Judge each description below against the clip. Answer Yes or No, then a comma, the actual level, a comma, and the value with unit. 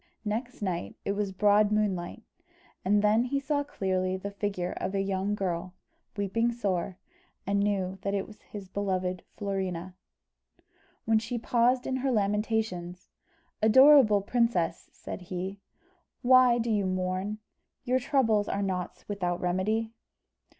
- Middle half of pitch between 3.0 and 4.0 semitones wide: Yes, average, 3.3 semitones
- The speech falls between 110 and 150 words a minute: Yes, slow, 135 wpm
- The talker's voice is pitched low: No, high, 200 Hz